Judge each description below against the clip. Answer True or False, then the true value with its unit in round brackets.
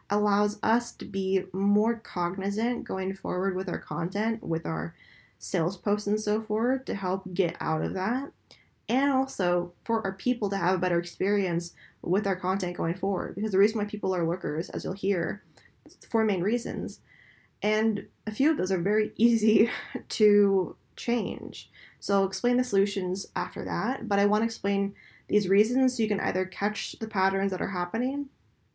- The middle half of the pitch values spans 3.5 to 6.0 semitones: False (2.9 semitones)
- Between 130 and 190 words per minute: True (180 wpm)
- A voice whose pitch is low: False (200 Hz)